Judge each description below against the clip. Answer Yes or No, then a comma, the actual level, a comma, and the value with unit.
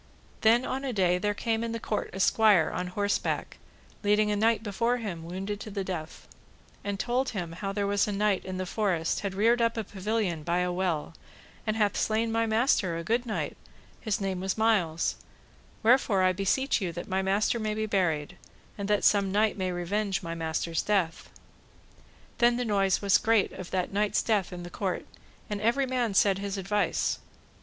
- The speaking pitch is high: Yes, high, 200 Hz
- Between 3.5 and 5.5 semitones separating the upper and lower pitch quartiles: No, average, 3.0 semitones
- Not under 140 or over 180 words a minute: No, average, 195 wpm